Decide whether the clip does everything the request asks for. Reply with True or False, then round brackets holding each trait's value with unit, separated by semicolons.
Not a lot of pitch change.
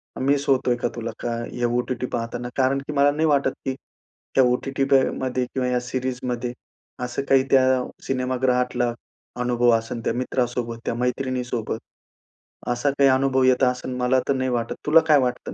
True (1.4 semitones)